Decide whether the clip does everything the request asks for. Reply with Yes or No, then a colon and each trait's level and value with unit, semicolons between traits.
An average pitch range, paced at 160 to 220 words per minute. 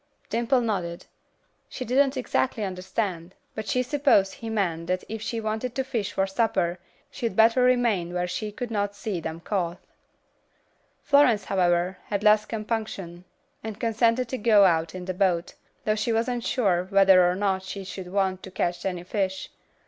Yes: average, 3.8 semitones; average, 170 wpm